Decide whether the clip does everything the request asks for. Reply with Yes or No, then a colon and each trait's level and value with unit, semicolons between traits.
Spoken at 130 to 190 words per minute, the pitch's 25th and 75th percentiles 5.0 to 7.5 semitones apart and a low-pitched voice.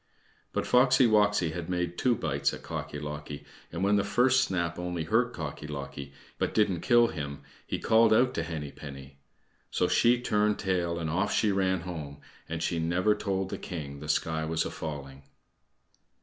Yes: average, 180 wpm; average, 5.3 semitones; very low, 85 Hz